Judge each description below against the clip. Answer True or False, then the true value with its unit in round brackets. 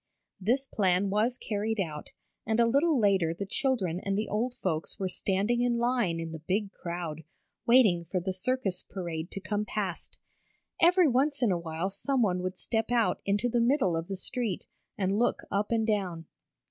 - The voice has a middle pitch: False (200 Hz)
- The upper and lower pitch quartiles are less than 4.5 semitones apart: False (4.8 semitones)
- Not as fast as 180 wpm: False (185 wpm)